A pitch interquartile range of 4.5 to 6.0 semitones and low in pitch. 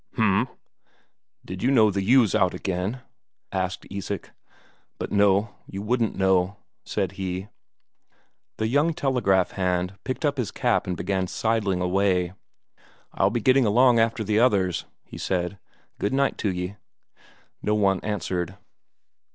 No: average, 3.6 semitones; low, 100 Hz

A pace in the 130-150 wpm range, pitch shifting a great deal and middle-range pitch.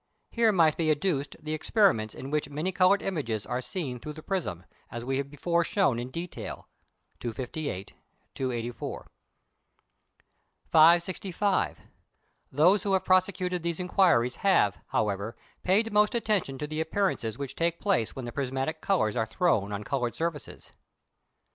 Yes: average, 145 wpm; wide, 6.8 semitones; medium, 155 Hz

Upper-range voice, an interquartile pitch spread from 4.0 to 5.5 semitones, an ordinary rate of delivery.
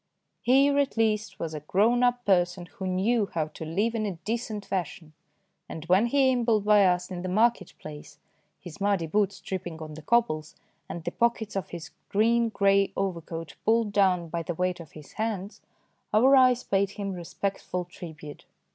Yes: high, 195 Hz; average, 4.6 semitones; average, 180 wpm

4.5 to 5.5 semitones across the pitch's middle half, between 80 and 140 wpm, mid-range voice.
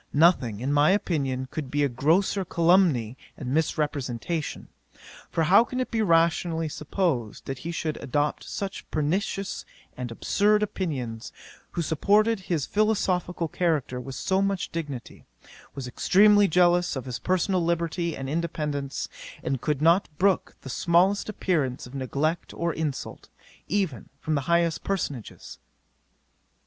Yes: average, 5.1 semitones; slow, 135 wpm; medium, 165 Hz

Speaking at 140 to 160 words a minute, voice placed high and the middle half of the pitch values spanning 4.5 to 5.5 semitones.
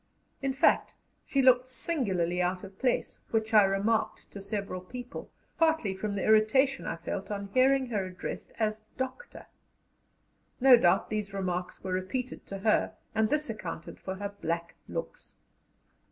Yes: average, 155 wpm; high, 215 Hz; average, 5.2 semitones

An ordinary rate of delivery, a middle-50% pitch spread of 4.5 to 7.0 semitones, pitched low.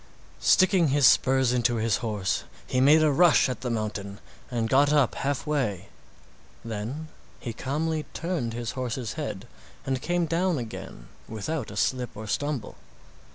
Yes: average, 150 wpm; average, 4.9 semitones; low, 130 Hz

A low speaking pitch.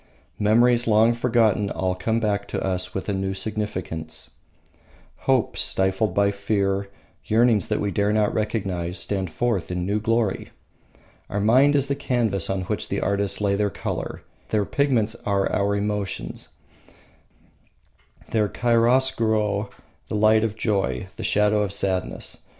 Yes: low, 105 Hz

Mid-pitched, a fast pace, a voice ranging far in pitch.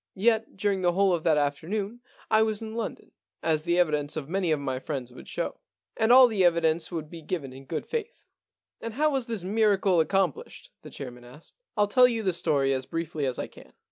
Yes: medium, 175 Hz; fast, 230 wpm; wide, 6.3 semitones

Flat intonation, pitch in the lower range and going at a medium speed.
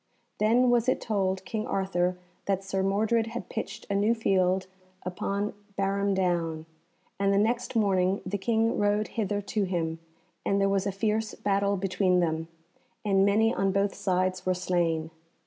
No: narrow, 2.2 semitones; high, 195 Hz; average, 165 wpm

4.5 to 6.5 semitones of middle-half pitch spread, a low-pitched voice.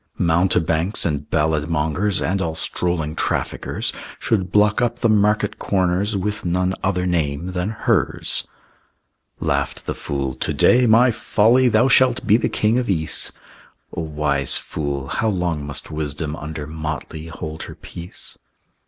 Yes: average, 5.1 semitones; very low, 90 Hz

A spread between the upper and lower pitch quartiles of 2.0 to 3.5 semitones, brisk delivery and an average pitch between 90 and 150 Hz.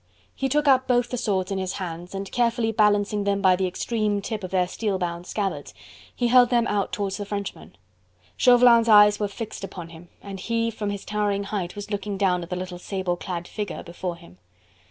No: average, 3.2 semitones; fast, 210 wpm; high, 200 Hz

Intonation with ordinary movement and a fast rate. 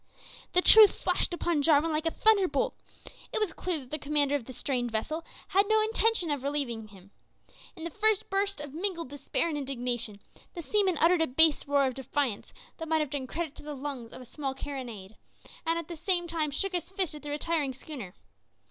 Yes: average, 4.3 semitones; fast, 210 wpm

